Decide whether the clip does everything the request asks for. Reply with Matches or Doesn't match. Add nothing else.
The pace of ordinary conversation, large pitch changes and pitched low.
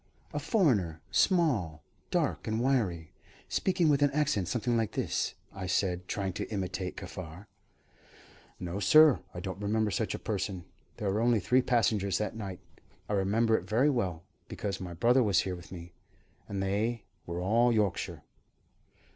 Doesn't match